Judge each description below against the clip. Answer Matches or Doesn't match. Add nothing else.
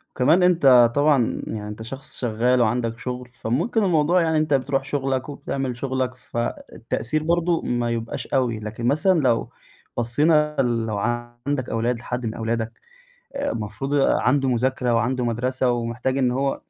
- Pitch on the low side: Matches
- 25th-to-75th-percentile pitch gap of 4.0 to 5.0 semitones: Doesn't match